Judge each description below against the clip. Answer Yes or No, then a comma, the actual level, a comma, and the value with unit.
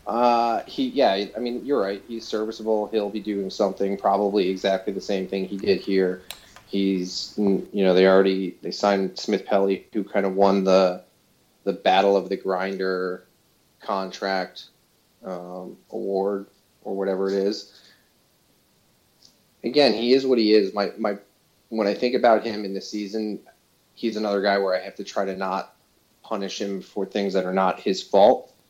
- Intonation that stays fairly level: Yes, narrow, 1.8 semitones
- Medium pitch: No, low, 100 Hz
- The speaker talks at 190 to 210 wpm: No, average, 170 wpm